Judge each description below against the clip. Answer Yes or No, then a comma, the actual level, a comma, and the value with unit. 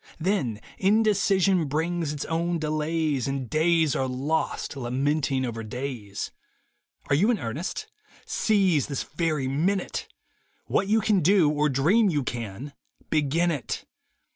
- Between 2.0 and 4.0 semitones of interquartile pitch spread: No, average, 4.6 semitones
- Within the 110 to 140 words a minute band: Yes, slow, 135 wpm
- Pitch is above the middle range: No, medium, 155 Hz